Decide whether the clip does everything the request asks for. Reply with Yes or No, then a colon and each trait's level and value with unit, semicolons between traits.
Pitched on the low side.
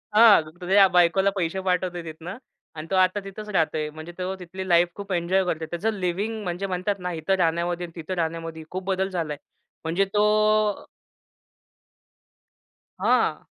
No: medium, 180 Hz